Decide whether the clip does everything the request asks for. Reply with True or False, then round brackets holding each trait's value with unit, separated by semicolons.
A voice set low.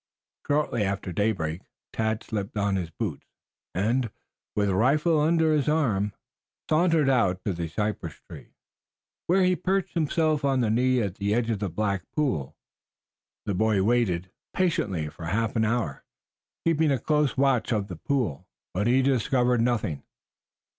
True (115 Hz)